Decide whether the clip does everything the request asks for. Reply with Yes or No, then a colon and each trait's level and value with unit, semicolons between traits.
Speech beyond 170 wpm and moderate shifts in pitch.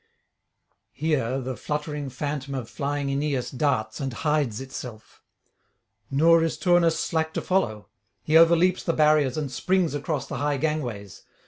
No: average, 140 wpm; average, 3.3 semitones